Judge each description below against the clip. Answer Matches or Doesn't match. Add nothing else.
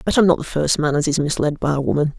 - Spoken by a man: Doesn't match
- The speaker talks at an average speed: Doesn't match